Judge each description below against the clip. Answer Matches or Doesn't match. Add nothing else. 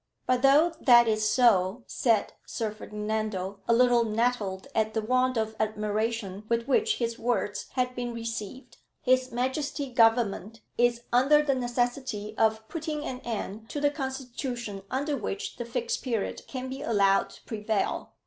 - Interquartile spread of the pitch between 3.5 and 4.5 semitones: Doesn't match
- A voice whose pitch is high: Matches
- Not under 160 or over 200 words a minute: Doesn't match